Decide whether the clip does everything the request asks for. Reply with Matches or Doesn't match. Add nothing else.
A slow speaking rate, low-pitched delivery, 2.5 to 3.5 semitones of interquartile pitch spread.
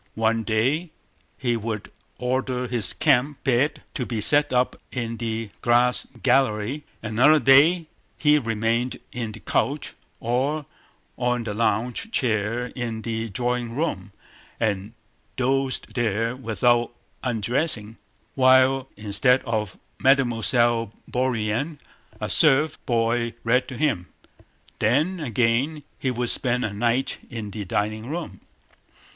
Matches